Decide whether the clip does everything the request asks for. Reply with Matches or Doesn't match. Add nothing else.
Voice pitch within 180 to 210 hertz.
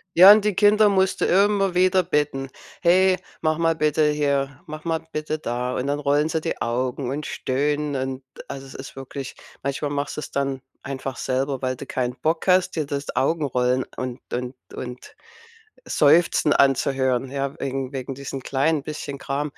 Doesn't match